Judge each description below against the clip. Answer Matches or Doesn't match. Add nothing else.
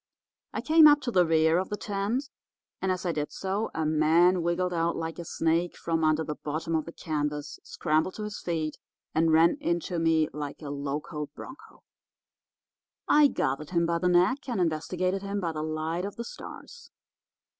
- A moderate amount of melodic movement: Matches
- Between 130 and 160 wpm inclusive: Doesn't match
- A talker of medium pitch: Matches